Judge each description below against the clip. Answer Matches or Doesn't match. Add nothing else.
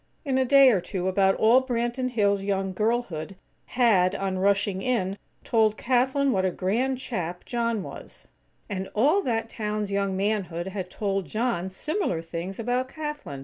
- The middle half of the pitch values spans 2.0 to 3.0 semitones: Doesn't match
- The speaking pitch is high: Matches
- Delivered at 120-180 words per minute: Matches